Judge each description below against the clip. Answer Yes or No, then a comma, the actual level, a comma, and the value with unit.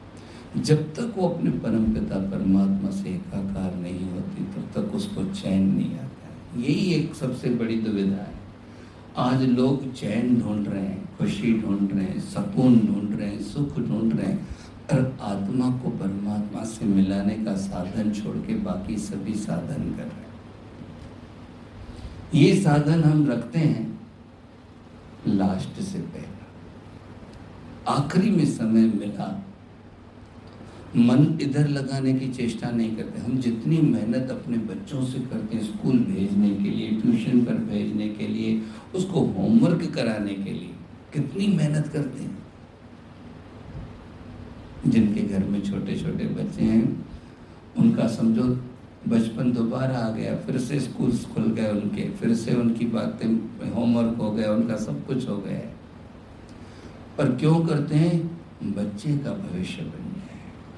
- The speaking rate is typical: Yes, average, 140 wpm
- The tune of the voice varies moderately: No, wide, 5.8 semitones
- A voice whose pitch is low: Yes, low, 115 Hz